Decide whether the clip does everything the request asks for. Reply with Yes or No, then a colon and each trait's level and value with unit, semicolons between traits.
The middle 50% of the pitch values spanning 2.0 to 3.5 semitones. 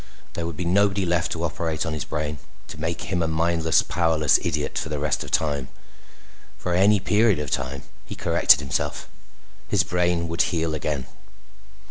Yes: narrow, 2.5 semitones